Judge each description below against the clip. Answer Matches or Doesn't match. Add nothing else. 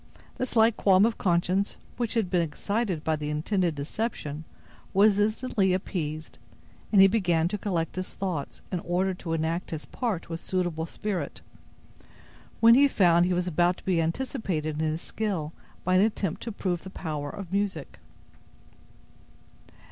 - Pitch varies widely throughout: Doesn't match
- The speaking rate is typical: Matches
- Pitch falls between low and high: Matches